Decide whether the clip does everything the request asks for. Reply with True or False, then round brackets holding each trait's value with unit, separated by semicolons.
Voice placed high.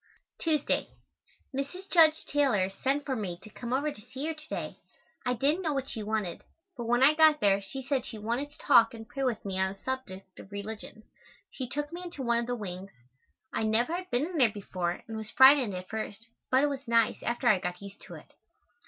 True (240 Hz)